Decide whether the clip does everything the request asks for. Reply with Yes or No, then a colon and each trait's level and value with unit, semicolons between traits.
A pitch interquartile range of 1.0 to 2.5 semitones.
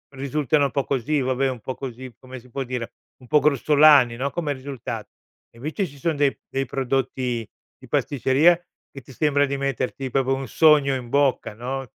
Yes: narrow, 1.9 semitones